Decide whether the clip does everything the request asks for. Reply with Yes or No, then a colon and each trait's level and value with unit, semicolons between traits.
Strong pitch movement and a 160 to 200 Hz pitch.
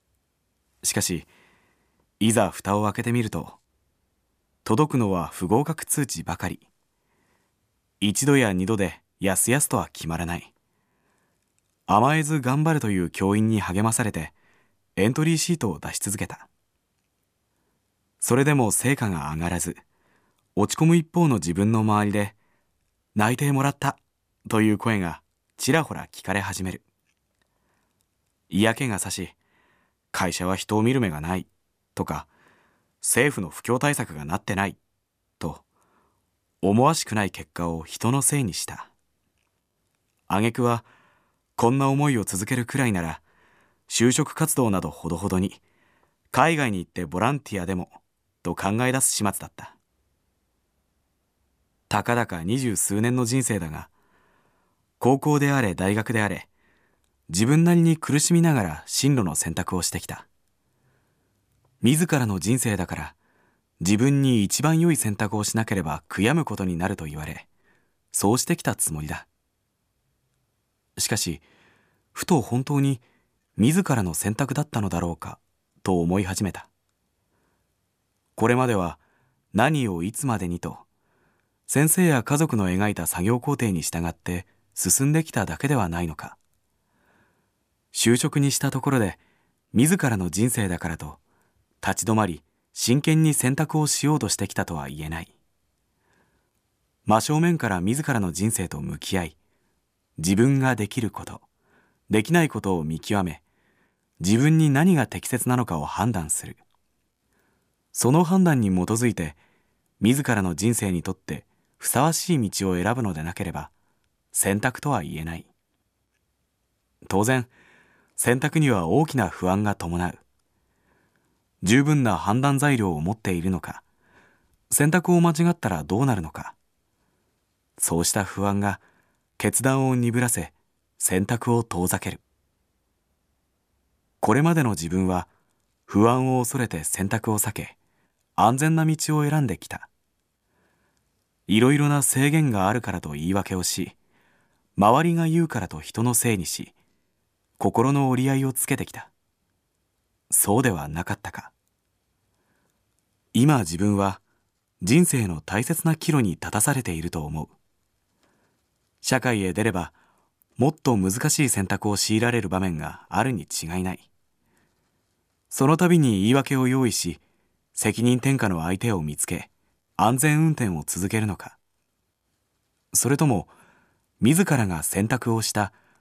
No: wide, 6.4 semitones; low, 105 Hz